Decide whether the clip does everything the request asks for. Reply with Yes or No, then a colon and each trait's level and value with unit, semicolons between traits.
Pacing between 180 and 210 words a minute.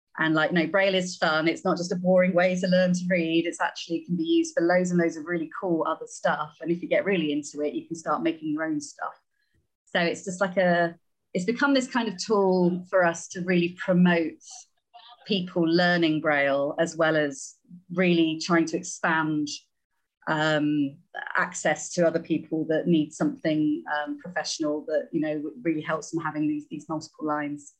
Yes: average, 200 wpm